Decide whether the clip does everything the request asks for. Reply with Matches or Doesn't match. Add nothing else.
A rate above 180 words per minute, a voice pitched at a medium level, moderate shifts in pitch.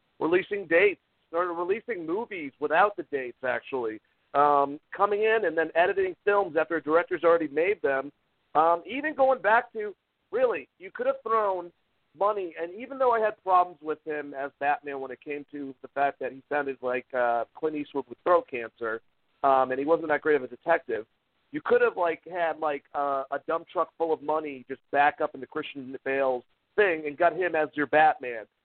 Doesn't match